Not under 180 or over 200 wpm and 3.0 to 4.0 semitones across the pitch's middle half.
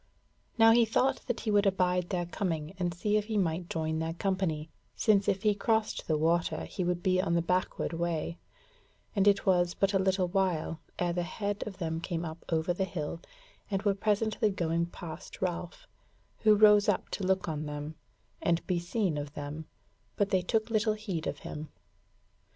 Yes: average, 190 wpm; average, 3.5 semitones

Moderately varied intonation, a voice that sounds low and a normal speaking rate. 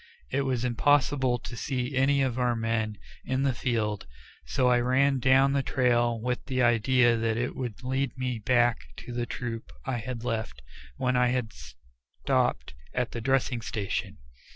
No: narrow, 2.3 semitones; low, 125 Hz; average, 170 wpm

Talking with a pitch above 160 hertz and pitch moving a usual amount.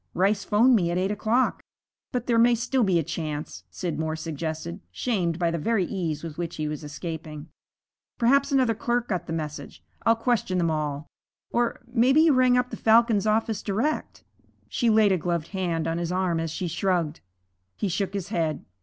No: medium, 185 Hz; wide, 5.9 semitones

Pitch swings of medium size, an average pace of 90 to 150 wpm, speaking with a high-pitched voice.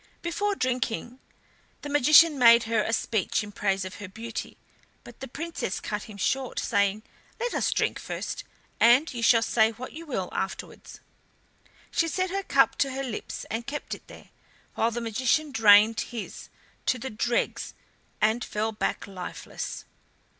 No: average, 4.1 semitones; average, 160 wpm; high, 235 Hz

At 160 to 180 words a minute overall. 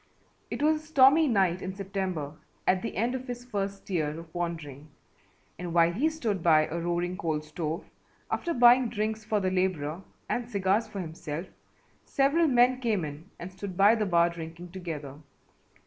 Yes: average, 175 wpm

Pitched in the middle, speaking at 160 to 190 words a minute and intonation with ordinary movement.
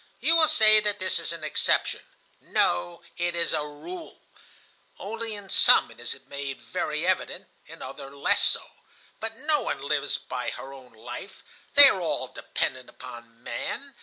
No: medium, 155 Hz; average, 165 wpm; wide, 8.7 semitones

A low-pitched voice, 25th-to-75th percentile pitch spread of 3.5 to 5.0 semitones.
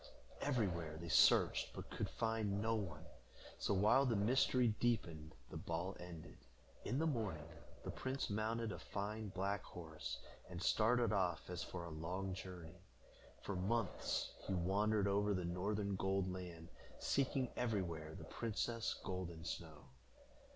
Yes: very low, 95 Hz; average, 4.3 semitones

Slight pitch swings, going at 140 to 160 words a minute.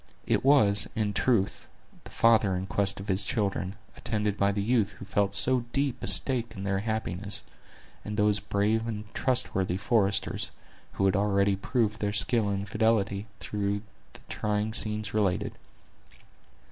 Yes: narrow, 1.9 semitones; average, 155 wpm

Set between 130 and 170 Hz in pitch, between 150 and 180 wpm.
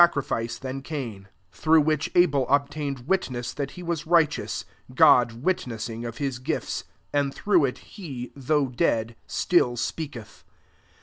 No: medium, 140 Hz; average, 140 wpm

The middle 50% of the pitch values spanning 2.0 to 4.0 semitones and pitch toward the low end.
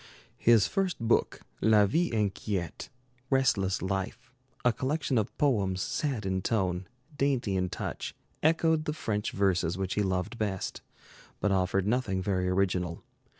No: average, 4.8 semitones; low, 105 Hz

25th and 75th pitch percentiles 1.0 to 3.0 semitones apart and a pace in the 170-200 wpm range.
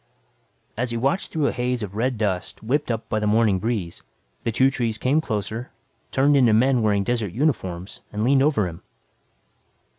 No: average, 3.8 semitones; average, 180 wpm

